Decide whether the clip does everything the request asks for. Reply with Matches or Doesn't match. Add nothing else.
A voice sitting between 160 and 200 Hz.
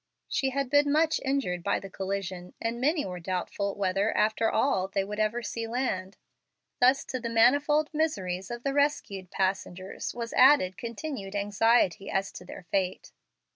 Doesn't match